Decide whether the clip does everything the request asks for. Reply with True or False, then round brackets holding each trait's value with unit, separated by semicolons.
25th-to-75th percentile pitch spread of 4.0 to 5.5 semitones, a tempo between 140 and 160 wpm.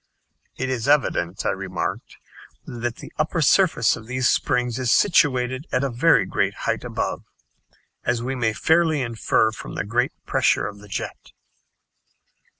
False (3.3 semitones; 155 wpm)